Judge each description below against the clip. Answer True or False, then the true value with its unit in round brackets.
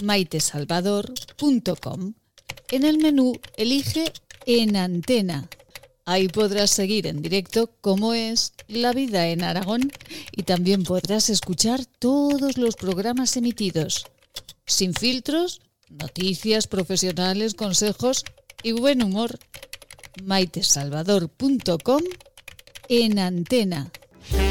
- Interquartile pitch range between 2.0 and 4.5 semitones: False (5.0 semitones)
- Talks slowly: True (90 wpm)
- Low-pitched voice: False (210 Hz)